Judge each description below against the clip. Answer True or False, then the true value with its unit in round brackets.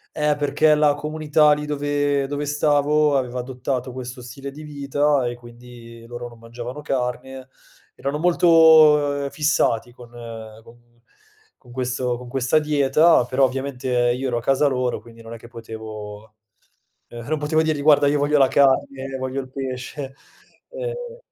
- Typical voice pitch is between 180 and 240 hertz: False (135 Hz)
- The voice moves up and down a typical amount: True (3.2 semitones)